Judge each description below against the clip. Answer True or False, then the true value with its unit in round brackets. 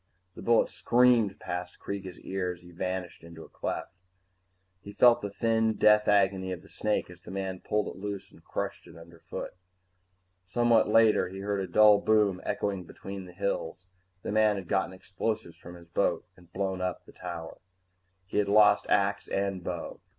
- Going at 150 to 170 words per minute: False (180 wpm)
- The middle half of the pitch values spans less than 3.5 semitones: True (2.6 semitones)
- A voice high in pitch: False (95 Hz)